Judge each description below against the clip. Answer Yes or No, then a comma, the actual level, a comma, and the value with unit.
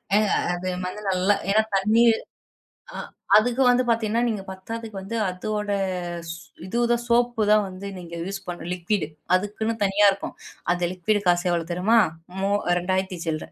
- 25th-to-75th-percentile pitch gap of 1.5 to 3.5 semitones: Yes, average, 3.2 semitones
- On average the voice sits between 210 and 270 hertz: No, high, 200 Hz